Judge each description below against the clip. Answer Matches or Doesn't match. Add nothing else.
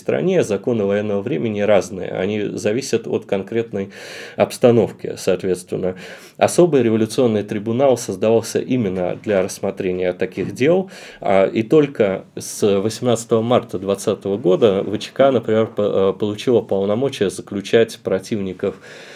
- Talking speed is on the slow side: Matches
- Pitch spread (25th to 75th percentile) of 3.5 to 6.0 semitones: Doesn't match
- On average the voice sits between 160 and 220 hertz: Doesn't match